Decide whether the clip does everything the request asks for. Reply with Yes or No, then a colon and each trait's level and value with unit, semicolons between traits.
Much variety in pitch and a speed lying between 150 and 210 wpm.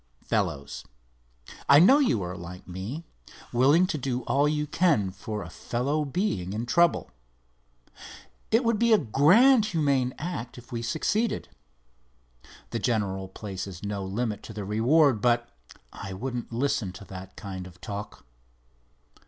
No: wide, 7.5 semitones; average, 140 wpm